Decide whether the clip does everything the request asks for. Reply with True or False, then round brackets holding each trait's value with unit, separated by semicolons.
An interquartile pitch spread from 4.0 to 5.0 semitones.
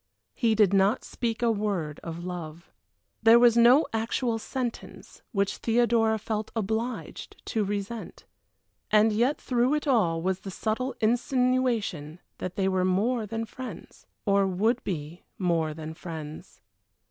True (4.4 semitones)